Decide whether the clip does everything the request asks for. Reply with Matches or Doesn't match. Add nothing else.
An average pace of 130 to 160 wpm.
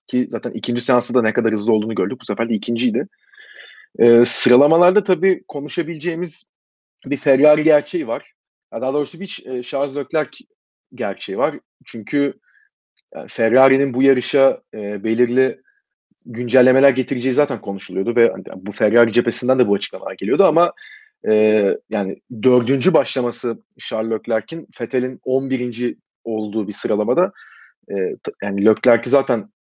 Matches